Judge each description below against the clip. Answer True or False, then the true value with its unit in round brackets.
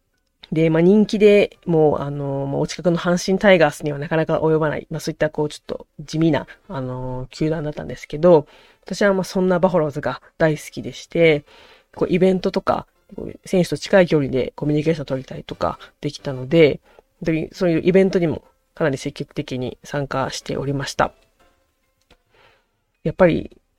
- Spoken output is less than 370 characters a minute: False (375 characters per minute)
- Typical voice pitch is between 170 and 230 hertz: False (155 Hz)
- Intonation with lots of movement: False (3.9 semitones)